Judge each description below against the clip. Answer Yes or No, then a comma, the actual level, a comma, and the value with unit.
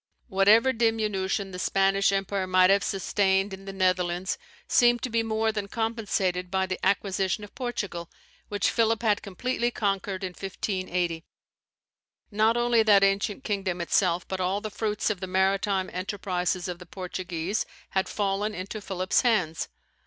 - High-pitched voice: Yes, high, 195 Hz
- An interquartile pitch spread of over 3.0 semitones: No, narrow, 2.5 semitones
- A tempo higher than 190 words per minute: No, average, 150 wpm